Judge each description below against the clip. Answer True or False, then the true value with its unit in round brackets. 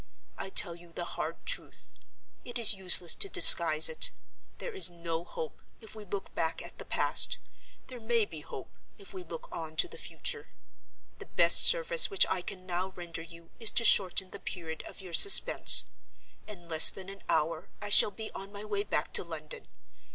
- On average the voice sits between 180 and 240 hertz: True (190 Hz)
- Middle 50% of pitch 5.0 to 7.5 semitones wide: False (4.6 semitones)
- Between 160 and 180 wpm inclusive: False (190 wpm)